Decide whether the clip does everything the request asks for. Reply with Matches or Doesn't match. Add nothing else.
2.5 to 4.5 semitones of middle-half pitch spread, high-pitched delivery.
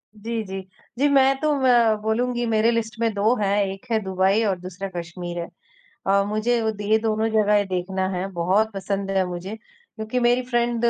Matches